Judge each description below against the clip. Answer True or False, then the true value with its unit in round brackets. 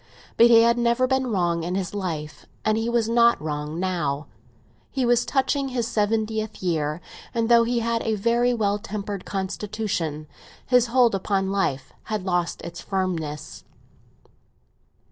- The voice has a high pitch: True (210 Hz)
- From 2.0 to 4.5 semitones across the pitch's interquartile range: False (4.9 semitones)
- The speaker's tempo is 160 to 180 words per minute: False (150 wpm)